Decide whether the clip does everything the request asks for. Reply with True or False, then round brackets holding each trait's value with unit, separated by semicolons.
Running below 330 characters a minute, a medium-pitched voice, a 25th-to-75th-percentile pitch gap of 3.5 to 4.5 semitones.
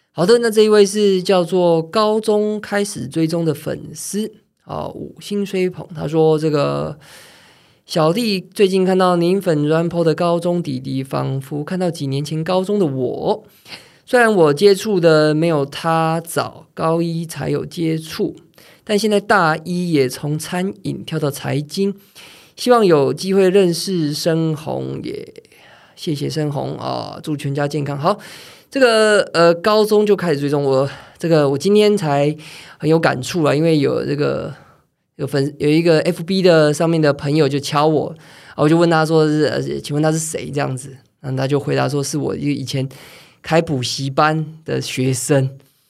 True (245 characters per minute; 160 Hz; 4.2 semitones)